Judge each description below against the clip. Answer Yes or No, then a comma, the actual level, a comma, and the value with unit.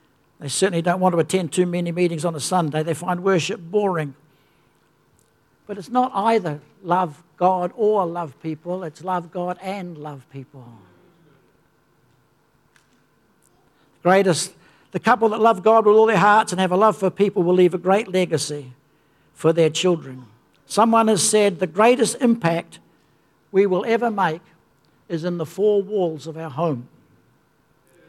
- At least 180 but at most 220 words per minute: No, average, 155 wpm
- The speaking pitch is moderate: Yes, medium, 180 Hz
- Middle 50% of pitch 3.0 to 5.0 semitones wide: Yes, average, 4.0 semitones